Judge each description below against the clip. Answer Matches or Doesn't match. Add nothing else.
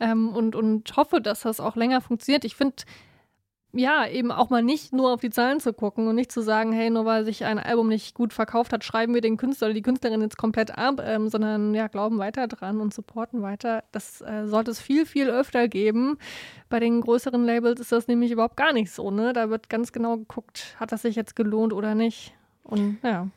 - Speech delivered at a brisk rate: Matches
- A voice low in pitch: Doesn't match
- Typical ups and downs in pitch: Doesn't match